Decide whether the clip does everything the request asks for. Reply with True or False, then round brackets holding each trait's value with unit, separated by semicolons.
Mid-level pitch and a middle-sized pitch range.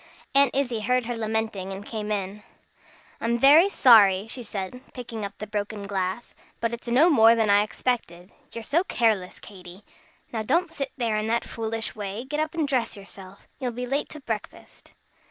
False (225 Hz; 3.5 semitones)